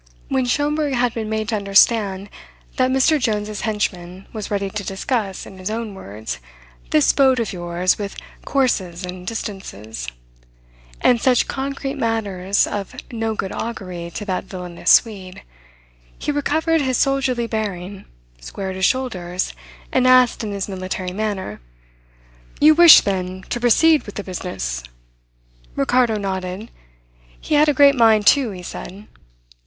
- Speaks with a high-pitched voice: Yes, high, 210 Hz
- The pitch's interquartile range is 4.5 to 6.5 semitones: Yes, average, 5.1 semitones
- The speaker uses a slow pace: No, average, 145 wpm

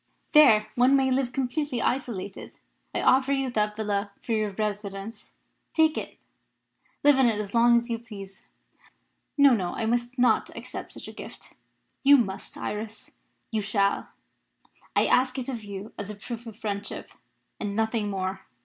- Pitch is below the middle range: No, high, 225 Hz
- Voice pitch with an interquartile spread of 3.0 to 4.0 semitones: Yes, average, 3.6 semitones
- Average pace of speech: Yes, average, 165 wpm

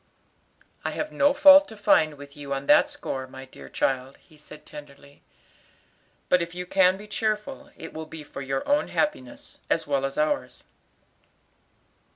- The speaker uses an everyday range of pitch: No, wide, 7.3 semitones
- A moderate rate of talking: Yes, average, 170 wpm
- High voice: No, medium, 155 Hz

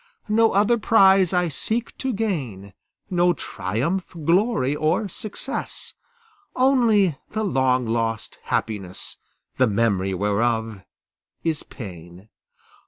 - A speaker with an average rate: No, slow, 105 wpm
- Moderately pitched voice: Yes, medium, 150 Hz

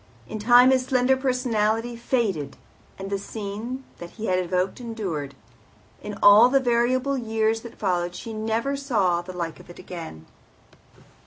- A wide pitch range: No, average, 5.0 semitones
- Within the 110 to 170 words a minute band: Yes, average, 150 wpm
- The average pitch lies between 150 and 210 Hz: No, high, 220 Hz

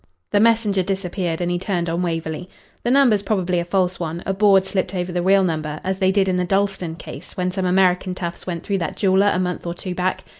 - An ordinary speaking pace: No, fast, 235 wpm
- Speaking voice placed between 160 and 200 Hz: Yes, medium, 185 Hz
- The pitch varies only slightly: Yes, narrow, 1.7 semitones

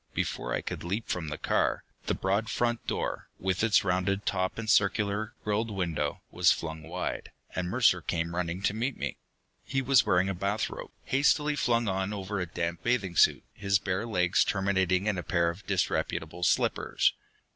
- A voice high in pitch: No, very low, 95 Hz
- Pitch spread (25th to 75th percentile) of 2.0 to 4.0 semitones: Yes, average, 3.4 semitones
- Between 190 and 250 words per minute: No, average, 180 wpm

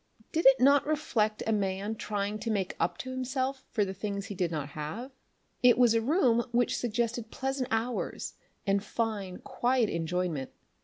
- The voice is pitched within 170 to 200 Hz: No, high, 225 Hz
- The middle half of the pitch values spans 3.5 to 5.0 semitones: Yes, average, 4.2 semitones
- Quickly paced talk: No, average, 170 wpm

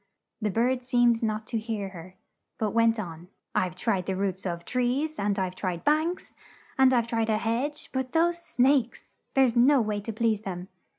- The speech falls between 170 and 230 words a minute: Yes, average, 185 wpm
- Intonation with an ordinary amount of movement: Yes, average, 4.4 semitones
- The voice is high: Yes, high, 225 Hz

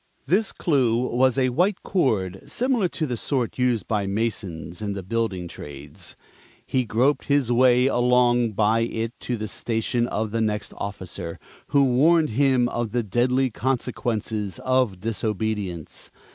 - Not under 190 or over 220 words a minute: No, average, 145 wpm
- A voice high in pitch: No, low, 115 Hz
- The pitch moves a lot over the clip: No, average, 3.6 semitones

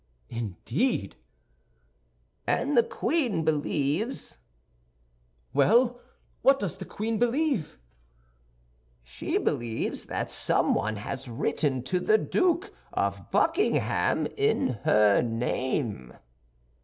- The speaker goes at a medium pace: No, slow, 90 wpm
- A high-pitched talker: No, medium, 165 Hz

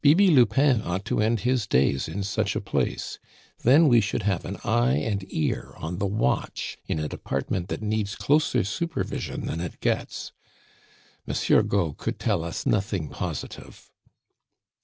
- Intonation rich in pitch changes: Yes, wide, 6.1 semitones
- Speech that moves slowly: No, average, 160 wpm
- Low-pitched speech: Yes, low, 100 Hz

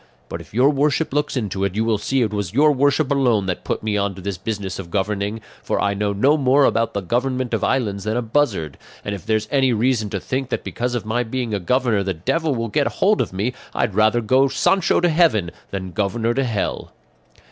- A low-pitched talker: Yes, low, 115 Hz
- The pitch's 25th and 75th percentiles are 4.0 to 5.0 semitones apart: Yes, average, 4.7 semitones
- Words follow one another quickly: Yes, fast, 235 wpm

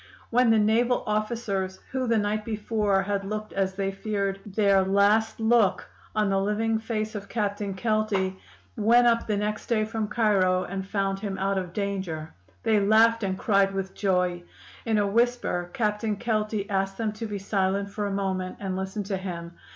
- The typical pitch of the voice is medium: No, high, 205 Hz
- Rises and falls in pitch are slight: Yes, narrow, 2.0 semitones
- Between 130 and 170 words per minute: No, average, 180 wpm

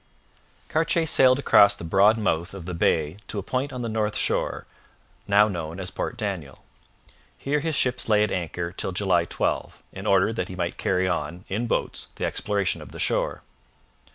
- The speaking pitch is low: Yes, low, 100 Hz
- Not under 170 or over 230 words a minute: Yes, average, 185 wpm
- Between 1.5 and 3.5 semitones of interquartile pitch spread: No, average, 4.2 semitones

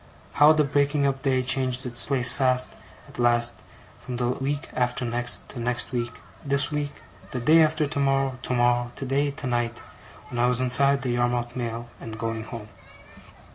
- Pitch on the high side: No, low, 125 Hz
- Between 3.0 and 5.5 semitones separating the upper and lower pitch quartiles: No, narrow, 2.4 semitones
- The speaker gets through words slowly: No, average, 170 wpm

